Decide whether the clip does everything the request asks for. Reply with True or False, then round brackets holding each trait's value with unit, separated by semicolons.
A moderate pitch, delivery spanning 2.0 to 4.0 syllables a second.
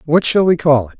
False (155 Hz; 6.0 syllables/s)